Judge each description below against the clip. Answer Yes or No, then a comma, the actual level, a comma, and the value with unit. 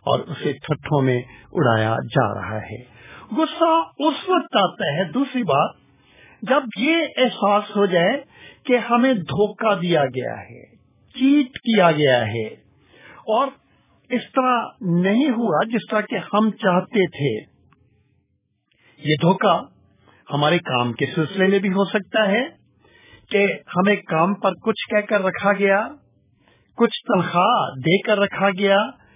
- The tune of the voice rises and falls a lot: Yes, wide, 6.7 semitones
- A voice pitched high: Yes, high, 200 Hz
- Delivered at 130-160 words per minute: Yes, average, 140 wpm